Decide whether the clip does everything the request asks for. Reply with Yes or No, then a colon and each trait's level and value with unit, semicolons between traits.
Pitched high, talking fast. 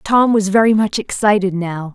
No: high, 200 Hz; average, 185 wpm